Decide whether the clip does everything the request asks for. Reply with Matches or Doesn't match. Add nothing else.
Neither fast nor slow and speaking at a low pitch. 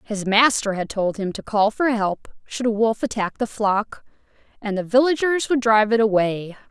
Doesn't match